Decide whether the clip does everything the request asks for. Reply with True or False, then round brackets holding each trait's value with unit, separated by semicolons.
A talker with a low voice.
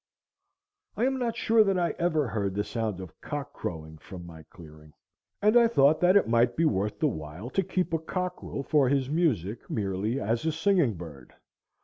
True (125 Hz)